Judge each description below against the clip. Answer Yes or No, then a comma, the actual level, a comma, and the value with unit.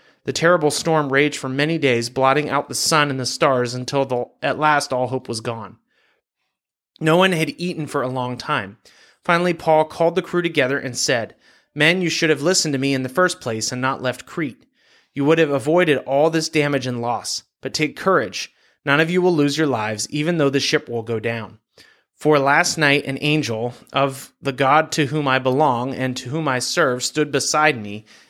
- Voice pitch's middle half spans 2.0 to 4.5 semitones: Yes, average, 3.4 semitones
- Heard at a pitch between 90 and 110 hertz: No, medium, 140 Hz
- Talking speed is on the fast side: Yes, fast, 210 wpm